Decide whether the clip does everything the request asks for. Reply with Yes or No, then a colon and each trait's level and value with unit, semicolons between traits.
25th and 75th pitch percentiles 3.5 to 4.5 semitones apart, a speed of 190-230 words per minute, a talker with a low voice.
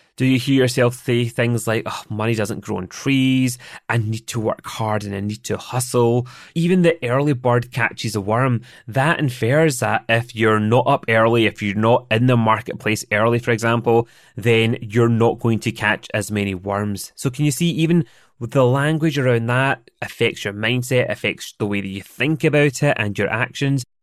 No: average, 3.1 semitones; average, 195 wpm; low, 120 Hz